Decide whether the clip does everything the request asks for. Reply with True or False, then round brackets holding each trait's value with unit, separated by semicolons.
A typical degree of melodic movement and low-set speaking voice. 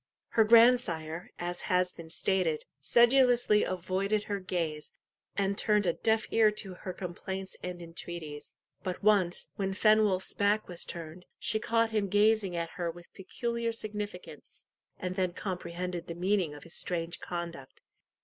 False (3.5 semitones; 185 Hz)